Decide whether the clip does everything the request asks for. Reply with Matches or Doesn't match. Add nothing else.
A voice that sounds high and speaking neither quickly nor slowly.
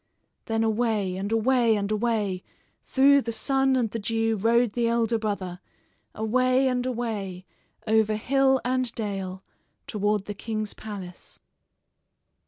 Doesn't match